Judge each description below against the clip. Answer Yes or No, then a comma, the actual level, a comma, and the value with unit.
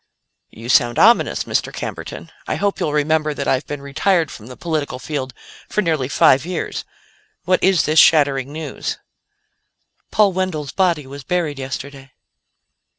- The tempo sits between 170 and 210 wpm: No, average, 150 wpm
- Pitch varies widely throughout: No, average, 4.2 semitones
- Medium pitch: Yes, medium, 150 Hz